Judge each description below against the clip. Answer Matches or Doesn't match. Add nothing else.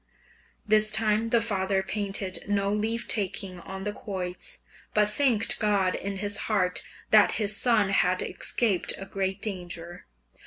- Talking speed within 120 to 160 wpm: Matches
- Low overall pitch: Doesn't match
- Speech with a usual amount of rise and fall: Doesn't match